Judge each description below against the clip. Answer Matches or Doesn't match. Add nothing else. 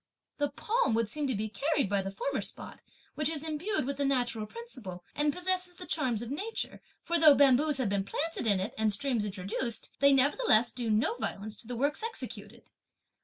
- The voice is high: Matches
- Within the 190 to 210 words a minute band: Matches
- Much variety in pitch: Matches